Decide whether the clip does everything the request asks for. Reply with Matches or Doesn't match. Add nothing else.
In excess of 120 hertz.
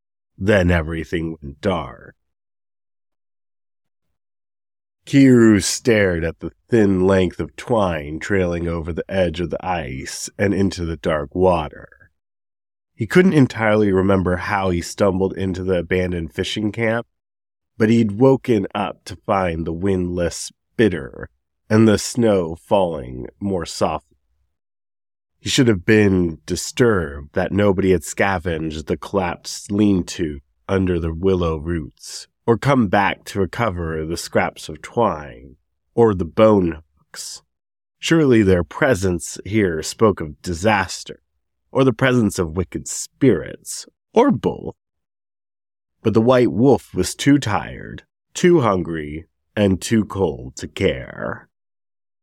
Doesn't match